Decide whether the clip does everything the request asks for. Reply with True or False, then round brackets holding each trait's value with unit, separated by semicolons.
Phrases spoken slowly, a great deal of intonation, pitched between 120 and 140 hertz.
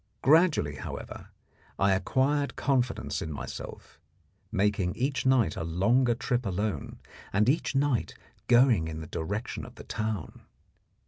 False (130 wpm; 5.7 semitones; 110 Hz)